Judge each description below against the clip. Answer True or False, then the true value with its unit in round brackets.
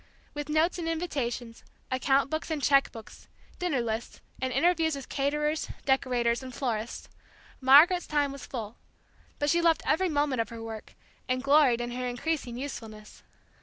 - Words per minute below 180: True (160 wpm)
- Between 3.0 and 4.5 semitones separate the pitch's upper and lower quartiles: True (4.2 semitones)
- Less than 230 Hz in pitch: False (275 Hz)